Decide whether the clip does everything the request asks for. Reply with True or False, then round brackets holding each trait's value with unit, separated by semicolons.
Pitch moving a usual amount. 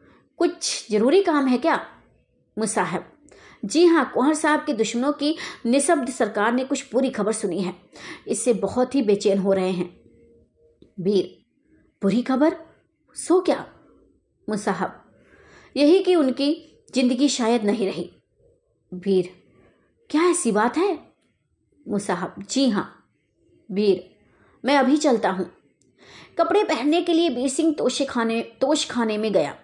False (6.9 semitones)